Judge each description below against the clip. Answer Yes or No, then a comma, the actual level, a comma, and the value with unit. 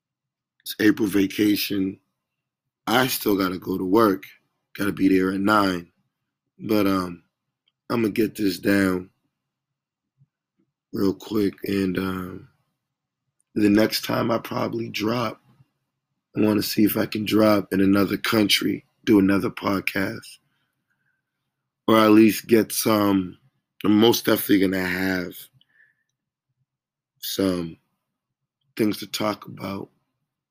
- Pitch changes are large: No, average, 4.6 semitones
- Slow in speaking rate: Yes, slow, 115 wpm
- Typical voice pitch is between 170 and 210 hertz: No, low, 105 Hz